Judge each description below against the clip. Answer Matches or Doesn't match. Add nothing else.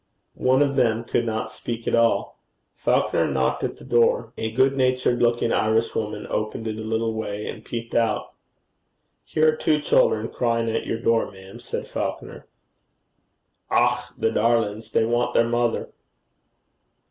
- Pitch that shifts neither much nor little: Doesn't match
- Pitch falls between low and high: Doesn't match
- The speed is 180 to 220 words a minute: Doesn't match